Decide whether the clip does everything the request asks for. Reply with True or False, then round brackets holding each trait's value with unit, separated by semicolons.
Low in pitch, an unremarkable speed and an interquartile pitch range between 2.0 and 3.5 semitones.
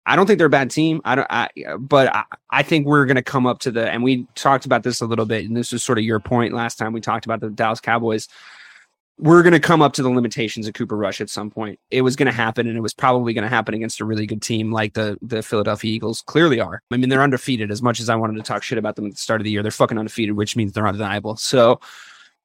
False (115 Hz; 295 wpm; 2.8 semitones)